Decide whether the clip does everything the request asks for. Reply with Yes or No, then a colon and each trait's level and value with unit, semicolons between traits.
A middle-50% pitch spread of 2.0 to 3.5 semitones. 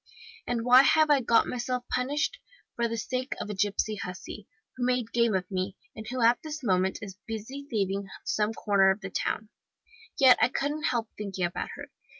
No: average, 4.1 semitones